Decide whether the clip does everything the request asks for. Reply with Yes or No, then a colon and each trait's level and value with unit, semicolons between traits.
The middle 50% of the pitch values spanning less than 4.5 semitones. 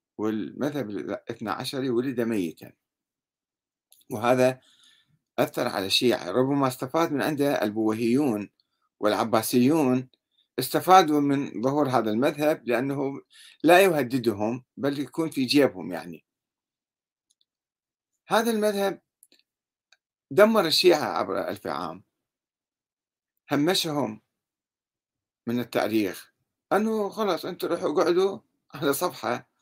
No: average, 5.3 semitones